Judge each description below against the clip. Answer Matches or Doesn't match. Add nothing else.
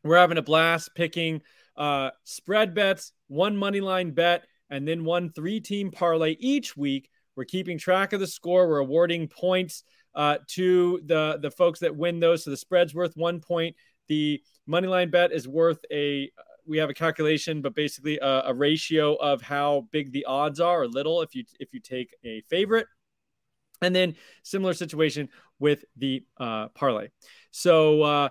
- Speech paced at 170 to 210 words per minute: Matches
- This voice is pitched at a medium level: Matches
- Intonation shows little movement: Doesn't match